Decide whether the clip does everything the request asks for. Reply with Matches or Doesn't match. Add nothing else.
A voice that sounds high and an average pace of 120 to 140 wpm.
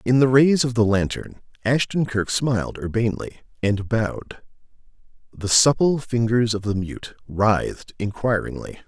Doesn't match